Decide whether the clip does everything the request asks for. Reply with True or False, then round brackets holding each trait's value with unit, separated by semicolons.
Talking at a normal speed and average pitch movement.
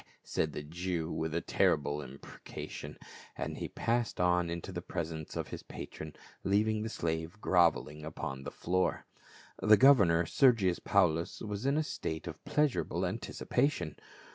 True (150 wpm; 4.7 semitones)